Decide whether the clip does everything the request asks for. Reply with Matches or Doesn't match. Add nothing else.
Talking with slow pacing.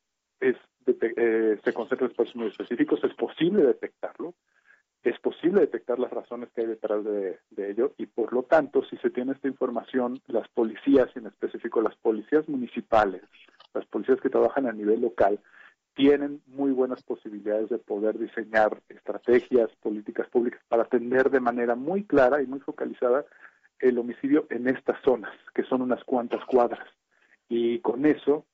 Doesn't match